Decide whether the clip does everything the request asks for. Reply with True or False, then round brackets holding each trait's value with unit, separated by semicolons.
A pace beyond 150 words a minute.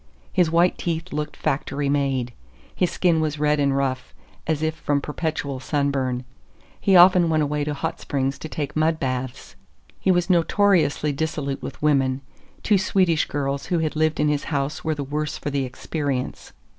True (175 wpm)